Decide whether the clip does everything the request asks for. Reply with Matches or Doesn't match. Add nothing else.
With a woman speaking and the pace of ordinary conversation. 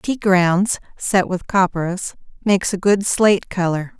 Matches